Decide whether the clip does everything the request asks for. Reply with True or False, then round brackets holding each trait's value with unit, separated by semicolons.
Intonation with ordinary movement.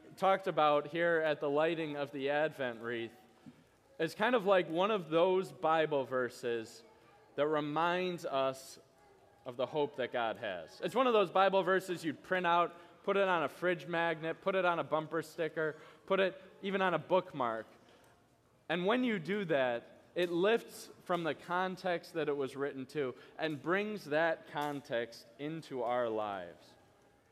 True (4.3 semitones)